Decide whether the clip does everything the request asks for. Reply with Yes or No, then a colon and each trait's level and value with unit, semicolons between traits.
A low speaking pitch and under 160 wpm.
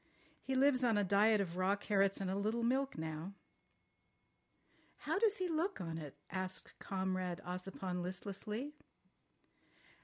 No: high, 195 Hz; average, 140 wpm